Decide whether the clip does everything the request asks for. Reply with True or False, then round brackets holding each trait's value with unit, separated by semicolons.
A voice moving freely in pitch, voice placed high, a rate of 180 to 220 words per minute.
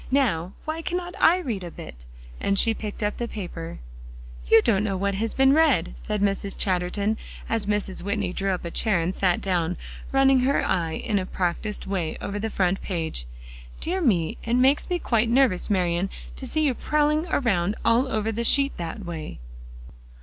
True (5.7 semitones; 205 Hz; 185 wpm)